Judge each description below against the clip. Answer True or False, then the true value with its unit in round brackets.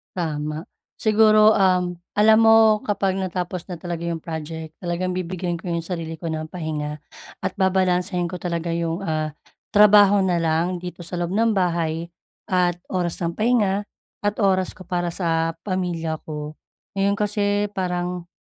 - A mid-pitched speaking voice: True (180 Hz)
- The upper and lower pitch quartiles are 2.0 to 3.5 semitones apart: True (2.7 semitones)